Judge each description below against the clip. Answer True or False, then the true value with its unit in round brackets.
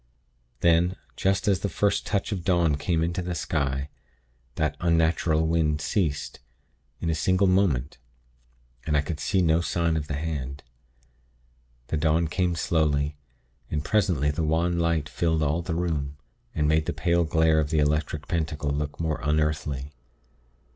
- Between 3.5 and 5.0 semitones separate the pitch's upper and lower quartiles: False (2.5 semitones)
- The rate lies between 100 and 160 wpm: True (155 wpm)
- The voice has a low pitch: True (80 Hz)